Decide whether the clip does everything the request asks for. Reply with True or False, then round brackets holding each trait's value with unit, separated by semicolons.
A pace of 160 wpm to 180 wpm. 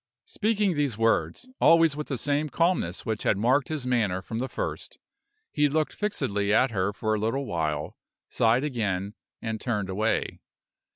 True (165 wpm)